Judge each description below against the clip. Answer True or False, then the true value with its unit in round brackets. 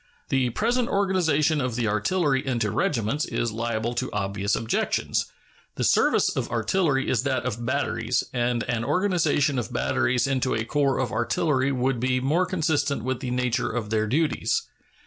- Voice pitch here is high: False (130 Hz)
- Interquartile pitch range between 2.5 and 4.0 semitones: True (3.7 semitones)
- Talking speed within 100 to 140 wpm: False (165 wpm)